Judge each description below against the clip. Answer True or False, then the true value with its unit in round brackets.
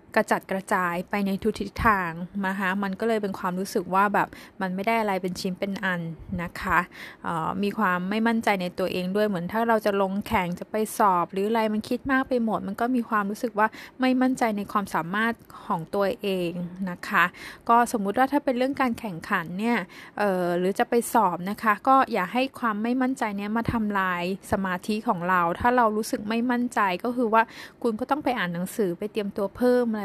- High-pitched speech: True (210 Hz)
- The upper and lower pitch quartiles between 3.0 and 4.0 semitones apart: True (3.5 semitones)